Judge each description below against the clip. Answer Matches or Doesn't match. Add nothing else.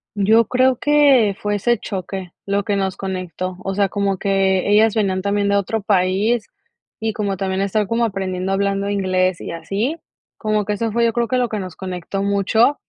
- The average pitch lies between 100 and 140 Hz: Doesn't match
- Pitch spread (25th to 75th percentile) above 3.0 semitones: Doesn't match